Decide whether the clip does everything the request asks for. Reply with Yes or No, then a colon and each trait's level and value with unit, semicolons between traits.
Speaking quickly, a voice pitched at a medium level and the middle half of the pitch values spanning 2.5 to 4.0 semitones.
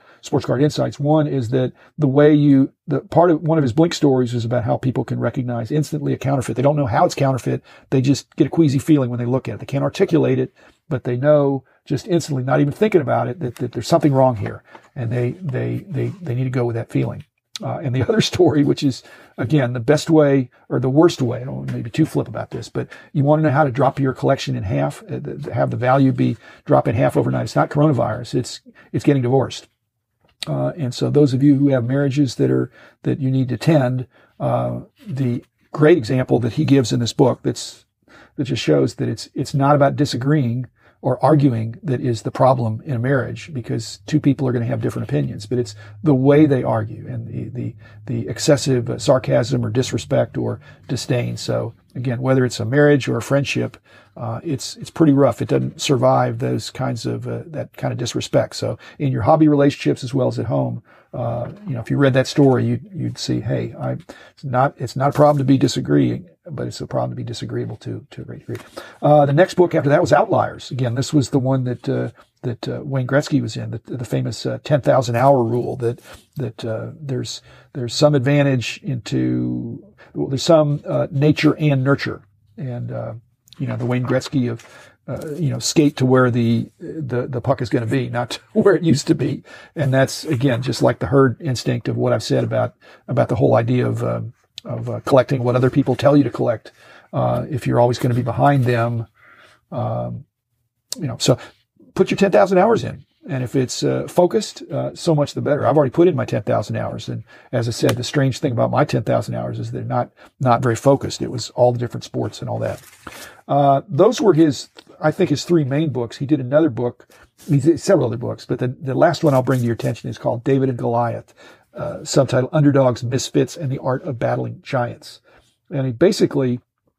No: fast, 225 wpm; low, 130 Hz; average, 3.3 semitones